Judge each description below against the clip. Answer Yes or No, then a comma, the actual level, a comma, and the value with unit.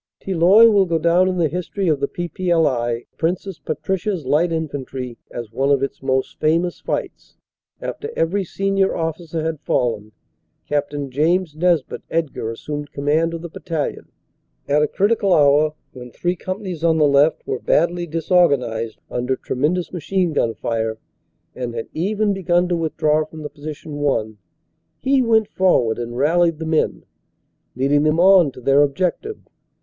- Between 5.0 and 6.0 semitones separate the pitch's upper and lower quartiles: No, average, 4.3 semitones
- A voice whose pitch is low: No, medium, 160 Hz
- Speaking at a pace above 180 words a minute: No, average, 150 wpm